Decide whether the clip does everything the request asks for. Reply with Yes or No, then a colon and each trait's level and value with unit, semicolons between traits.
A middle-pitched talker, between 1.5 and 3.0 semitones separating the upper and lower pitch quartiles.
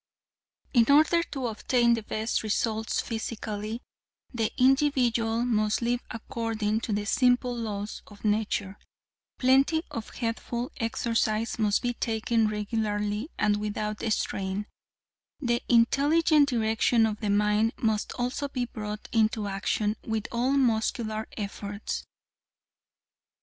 No: high, 225 Hz; narrow, 2.4 semitones